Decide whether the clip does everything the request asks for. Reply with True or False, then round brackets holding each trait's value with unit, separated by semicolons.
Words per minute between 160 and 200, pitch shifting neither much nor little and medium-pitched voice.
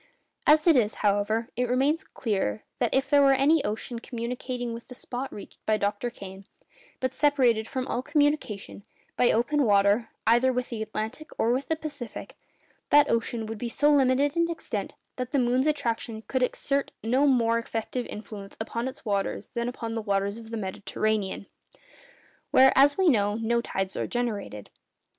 False (165 wpm; 3.7 semitones; 240 Hz)